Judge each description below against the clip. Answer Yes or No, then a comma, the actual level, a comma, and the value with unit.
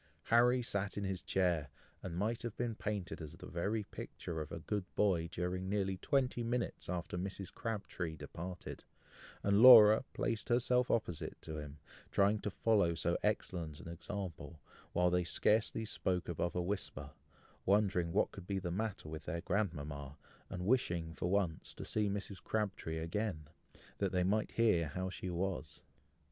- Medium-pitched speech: No, very low, 95 Hz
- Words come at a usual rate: Yes, average, 165 wpm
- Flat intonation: No, average, 3.8 semitones